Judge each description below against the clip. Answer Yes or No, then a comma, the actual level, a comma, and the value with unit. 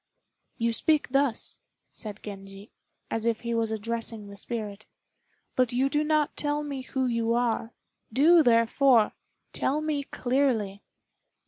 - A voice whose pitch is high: Yes, high, 235 Hz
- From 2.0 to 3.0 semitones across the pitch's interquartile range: No, average, 4.0 semitones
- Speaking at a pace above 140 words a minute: No, slow, 135 wpm